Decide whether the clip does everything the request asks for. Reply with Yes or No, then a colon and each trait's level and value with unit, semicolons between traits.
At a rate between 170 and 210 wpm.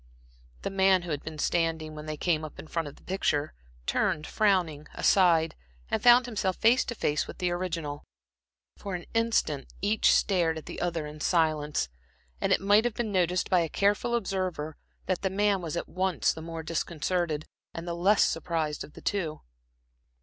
Yes: average, 185 wpm